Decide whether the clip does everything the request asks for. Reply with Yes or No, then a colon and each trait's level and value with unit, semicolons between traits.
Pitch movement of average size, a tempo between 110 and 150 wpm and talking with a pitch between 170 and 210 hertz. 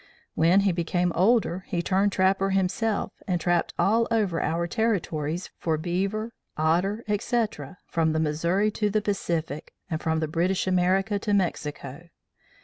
Yes: average, 3.6 semitones; average, 140 wpm; medium, 185 Hz